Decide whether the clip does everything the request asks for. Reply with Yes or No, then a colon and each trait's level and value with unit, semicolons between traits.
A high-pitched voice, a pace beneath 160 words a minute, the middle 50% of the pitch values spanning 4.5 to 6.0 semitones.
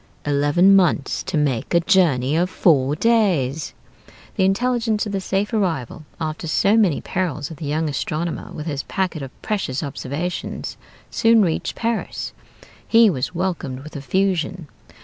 No: medium, 170 Hz; average, 150 wpm; average, 4.9 semitones